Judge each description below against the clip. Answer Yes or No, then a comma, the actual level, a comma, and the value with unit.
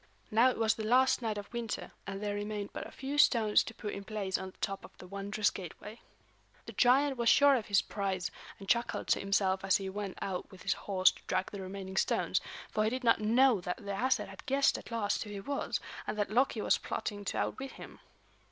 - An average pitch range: Yes, average, 3.2 semitones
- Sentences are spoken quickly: Yes, fast, 235 wpm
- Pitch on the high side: Yes, high, 210 Hz